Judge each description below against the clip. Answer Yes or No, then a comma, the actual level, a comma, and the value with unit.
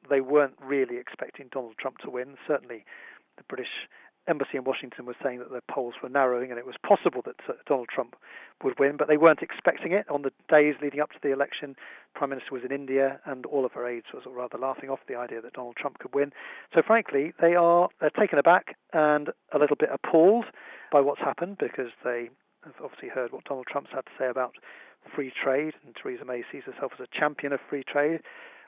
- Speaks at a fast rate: Yes, fast, 220 wpm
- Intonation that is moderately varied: No, narrow, 2.3 semitones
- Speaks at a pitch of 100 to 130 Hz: No, medium, 140 Hz